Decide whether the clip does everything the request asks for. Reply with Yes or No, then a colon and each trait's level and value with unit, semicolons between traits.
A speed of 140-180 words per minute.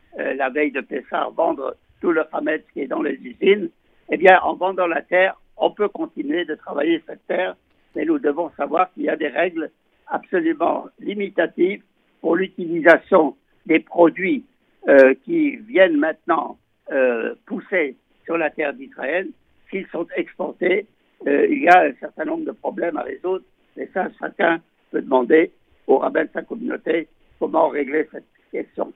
Yes: average, 165 wpm